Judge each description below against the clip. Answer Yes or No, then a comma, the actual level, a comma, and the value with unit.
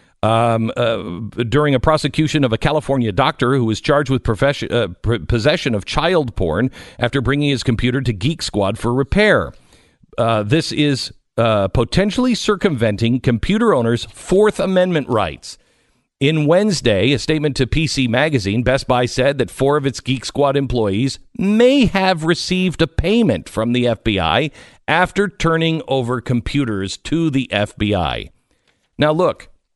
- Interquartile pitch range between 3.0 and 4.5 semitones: No, average, 5.1 semitones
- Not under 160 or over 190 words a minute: No, average, 145 wpm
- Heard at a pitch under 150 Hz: Yes, low, 135 Hz